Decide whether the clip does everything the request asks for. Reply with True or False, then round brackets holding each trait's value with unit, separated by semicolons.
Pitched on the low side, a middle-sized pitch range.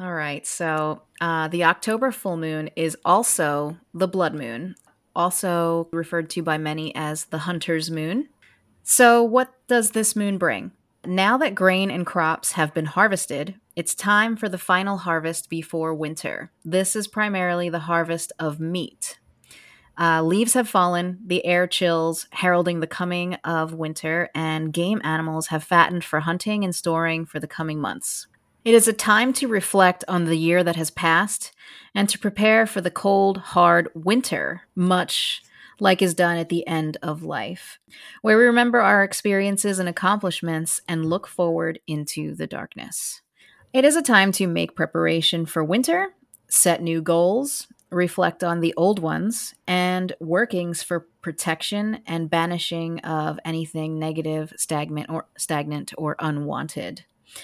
False (175 Hz; 3.5 semitones)